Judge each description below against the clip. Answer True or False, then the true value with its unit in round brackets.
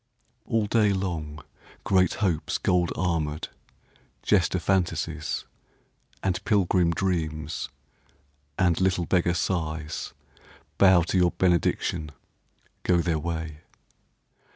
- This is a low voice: True (85 Hz)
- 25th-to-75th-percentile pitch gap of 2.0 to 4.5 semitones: True (2.7 semitones)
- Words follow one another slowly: True (95 wpm)